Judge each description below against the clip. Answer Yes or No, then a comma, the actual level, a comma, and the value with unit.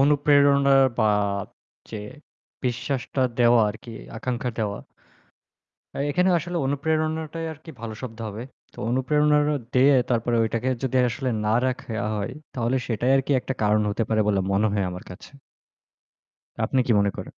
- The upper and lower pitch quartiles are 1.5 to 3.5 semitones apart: No, average, 4.2 semitones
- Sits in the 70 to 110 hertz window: No, low, 125 Hz